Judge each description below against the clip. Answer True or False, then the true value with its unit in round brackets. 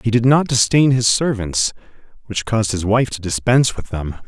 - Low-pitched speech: True (110 Hz)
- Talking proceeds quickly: False (195 wpm)